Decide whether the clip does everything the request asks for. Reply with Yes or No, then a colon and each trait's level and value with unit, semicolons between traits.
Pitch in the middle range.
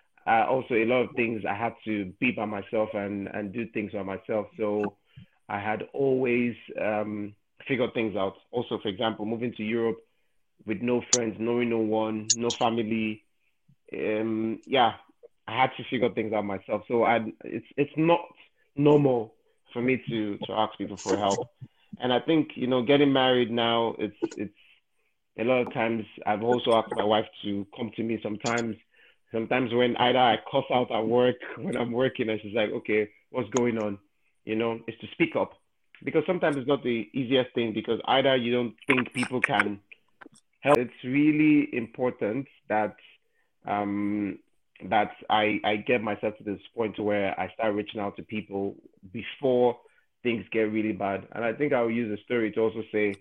No: low, 115 Hz